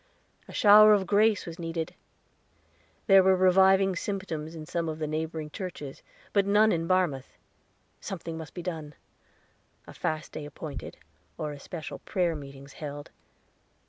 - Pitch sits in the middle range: Yes, medium, 165 Hz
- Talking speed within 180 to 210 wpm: No, average, 145 wpm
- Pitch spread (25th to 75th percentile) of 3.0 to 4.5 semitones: Yes, average, 3.7 semitones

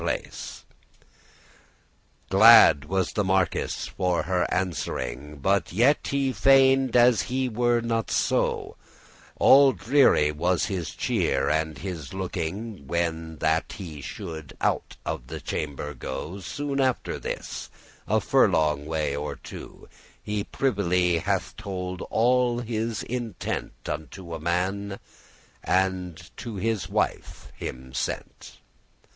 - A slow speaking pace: Yes, slow, 120 wpm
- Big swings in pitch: Yes, wide, 6.3 semitones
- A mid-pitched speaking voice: No, very low, 95 Hz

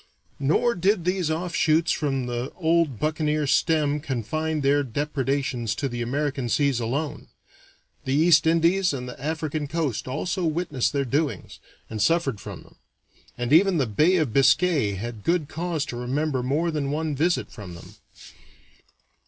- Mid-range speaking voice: Yes, medium, 150 Hz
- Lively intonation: No, average, 3.8 semitones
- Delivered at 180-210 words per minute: No, average, 150 wpm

